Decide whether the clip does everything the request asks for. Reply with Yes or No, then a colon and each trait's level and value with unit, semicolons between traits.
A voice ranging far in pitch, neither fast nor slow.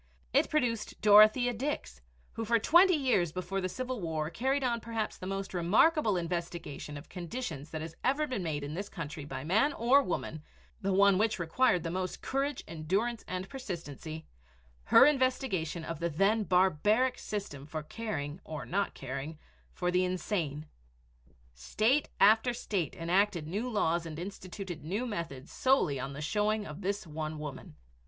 Yes: wide, 6.1 semitones; average, 160 wpm